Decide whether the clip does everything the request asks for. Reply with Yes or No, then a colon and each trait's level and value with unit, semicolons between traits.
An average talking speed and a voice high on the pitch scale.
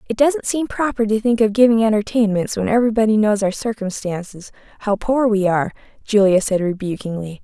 Yes: average, 160 wpm; high, 215 Hz